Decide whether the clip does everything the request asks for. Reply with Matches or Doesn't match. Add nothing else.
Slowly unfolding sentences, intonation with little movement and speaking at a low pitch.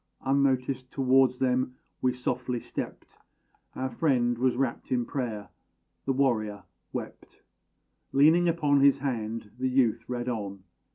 Matches